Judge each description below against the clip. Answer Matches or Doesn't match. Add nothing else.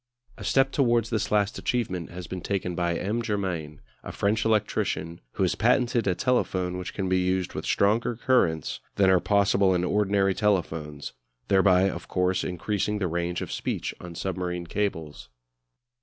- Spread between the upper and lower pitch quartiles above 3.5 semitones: Doesn't match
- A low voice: Matches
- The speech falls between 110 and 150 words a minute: Doesn't match